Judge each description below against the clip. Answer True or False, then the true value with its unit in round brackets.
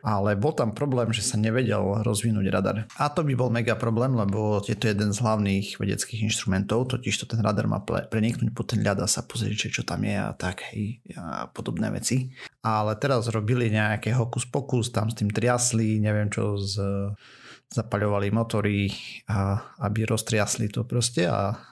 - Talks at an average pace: False (175 wpm)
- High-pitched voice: False (110 Hz)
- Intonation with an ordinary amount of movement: False (2.3 semitones)